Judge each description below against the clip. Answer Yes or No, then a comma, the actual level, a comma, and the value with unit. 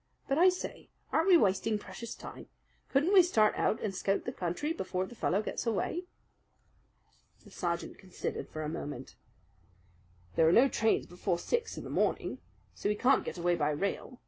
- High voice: Yes, high, 210 Hz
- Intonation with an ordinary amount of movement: No, wide, 7.5 semitones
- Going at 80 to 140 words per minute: No, average, 180 wpm